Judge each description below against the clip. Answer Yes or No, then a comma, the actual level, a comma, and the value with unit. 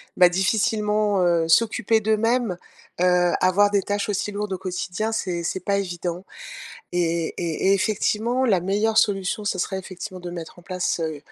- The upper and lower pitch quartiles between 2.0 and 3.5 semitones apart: Yes, average, 2.9 semitones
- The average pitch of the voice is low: No, high, 190 Hz